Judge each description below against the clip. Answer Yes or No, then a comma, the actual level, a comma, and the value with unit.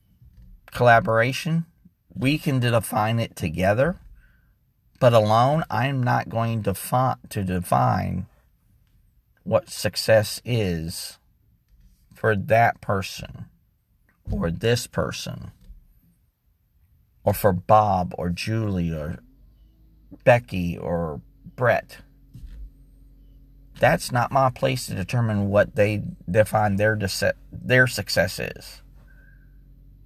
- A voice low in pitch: Yes, low, 110 Hz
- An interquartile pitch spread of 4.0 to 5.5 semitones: Yes, average, 4.8 semitones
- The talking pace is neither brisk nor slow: No, slow, 95 wpm